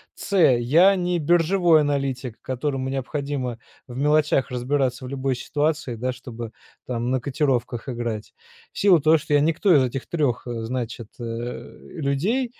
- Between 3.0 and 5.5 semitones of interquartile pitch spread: Yes, average, 3.9 semitones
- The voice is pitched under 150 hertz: Yes, low, 135 Hz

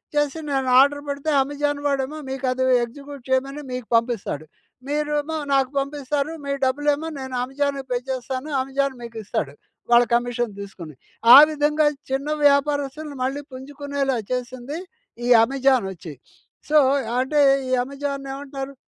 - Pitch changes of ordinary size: No, narrow, 2.0 semitones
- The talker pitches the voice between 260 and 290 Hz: Yes, very high, 275 Hz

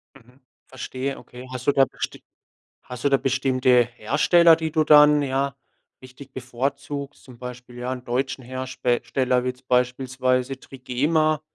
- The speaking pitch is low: Yes, low, 130 Hz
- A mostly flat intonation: Yes, narrow, 1.8 semitones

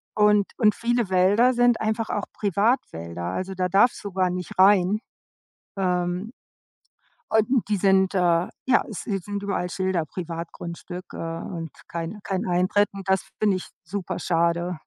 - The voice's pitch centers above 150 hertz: Yes, high, 190 Hz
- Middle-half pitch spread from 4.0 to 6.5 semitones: No, average, 2.7 semitones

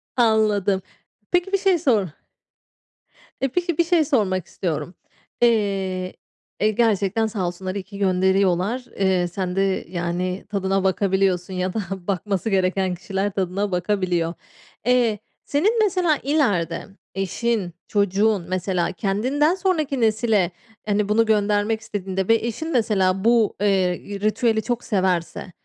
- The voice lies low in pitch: No, high, 200 Hz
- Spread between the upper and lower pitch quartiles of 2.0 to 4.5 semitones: Yes, average, 3.5 semitones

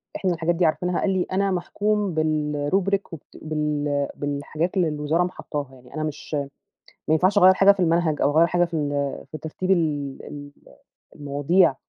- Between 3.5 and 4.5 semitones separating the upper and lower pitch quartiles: Yes, average, 3.8 semitones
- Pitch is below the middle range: No, medium, 160 Hz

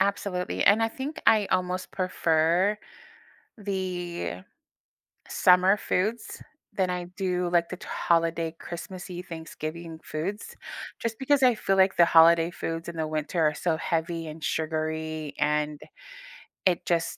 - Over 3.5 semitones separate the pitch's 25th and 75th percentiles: No, average, 2.8 semitones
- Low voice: No, medium, 175 Hz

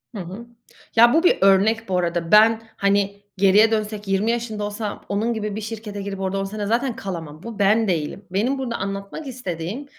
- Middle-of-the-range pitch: No, high, 205 Hz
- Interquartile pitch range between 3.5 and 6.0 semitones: No, narrow, 2.6 semitones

